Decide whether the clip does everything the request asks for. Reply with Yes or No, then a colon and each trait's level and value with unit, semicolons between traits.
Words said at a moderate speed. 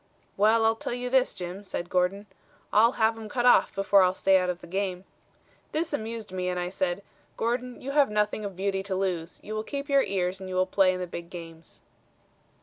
No: fast, 225 wpm